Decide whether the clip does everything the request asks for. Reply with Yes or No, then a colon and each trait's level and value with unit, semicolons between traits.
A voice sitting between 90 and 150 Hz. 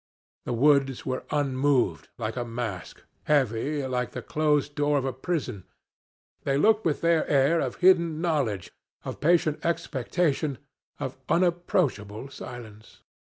Yes: medium, 140 Hz